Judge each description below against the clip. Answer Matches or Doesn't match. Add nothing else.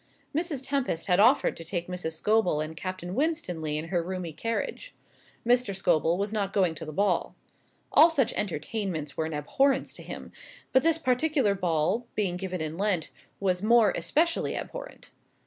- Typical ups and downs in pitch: Doesn't match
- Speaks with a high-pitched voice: Matches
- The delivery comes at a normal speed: Matches